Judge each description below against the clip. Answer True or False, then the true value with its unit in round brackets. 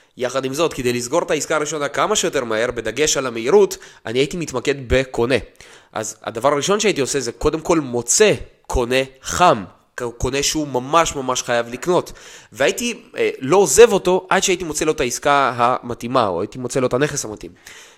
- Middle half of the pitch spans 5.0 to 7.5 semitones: True (5.6 semitones)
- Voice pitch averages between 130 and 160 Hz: True (140 Hz)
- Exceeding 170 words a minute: True (180 wpm)